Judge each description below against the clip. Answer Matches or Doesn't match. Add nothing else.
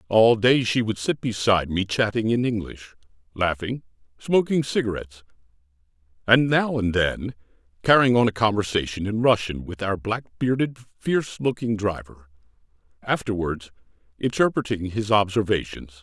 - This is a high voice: Doesn't match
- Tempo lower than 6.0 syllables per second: Matches